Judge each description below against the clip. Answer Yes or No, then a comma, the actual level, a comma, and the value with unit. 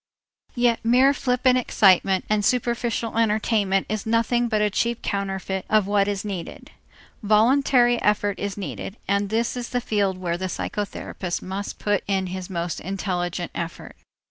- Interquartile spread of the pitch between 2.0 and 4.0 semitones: Yes, average, 3.4 semitones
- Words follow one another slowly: No, average, 150 wpm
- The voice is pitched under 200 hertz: No, high, 205 Hz